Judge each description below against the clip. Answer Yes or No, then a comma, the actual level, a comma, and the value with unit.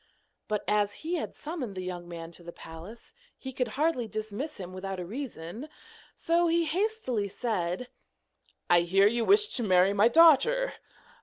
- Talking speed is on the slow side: No, average, 165 wpm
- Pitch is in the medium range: No, high, 220 Hz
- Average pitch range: No, wide, 8.8 semitones